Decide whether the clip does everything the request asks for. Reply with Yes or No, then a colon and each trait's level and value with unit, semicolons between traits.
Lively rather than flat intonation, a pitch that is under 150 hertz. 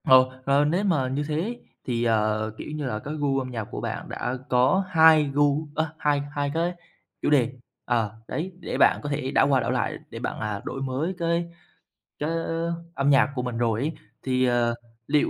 No: average, 3.7 semitones; medium, 140 Hz